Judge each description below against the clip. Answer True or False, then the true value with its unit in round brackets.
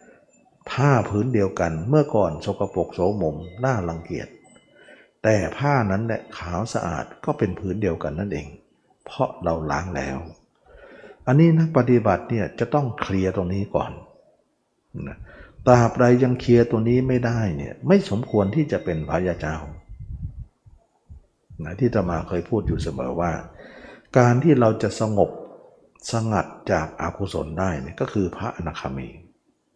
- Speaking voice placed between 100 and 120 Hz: True (105 Hz)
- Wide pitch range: True (6.2 semitones)